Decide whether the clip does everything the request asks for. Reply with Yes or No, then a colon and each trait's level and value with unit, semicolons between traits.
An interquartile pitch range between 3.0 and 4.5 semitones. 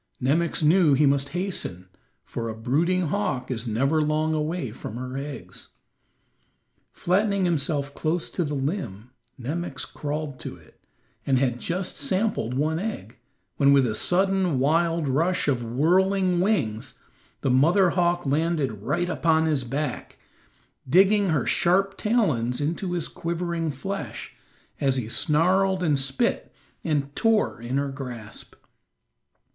No: average, 4.9 semitones